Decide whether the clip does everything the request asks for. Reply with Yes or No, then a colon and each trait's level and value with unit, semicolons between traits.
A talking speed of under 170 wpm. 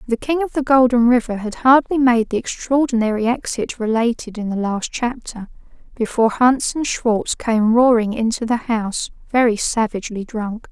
Yes: average, 160 wpm